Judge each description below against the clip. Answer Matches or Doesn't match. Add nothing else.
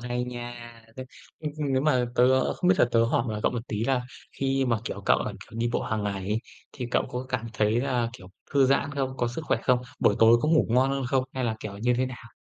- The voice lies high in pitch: Doesn't match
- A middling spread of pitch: Doesn't match